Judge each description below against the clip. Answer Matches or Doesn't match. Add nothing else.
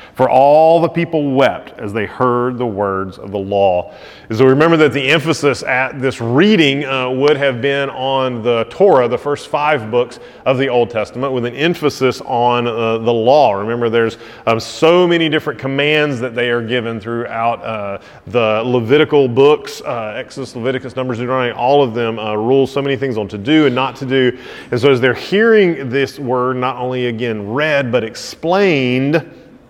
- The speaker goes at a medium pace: Matches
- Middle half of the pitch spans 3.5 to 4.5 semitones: Doesn't match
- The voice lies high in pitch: Doesn't match